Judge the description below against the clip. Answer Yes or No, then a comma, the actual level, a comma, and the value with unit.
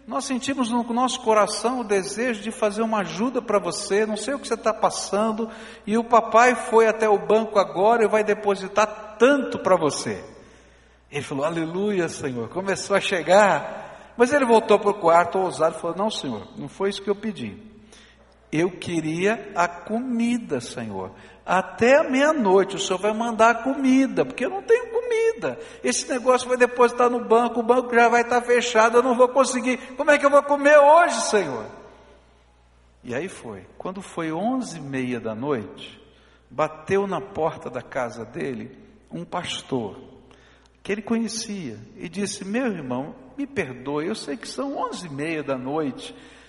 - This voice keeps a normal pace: Yes, average, 175 wpm